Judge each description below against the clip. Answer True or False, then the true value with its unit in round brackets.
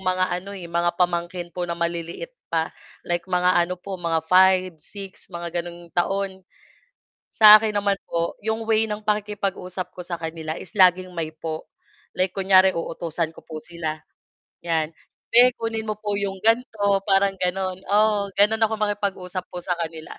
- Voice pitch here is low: False (185 Hz)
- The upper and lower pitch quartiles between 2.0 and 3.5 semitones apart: True (2.9 semitones)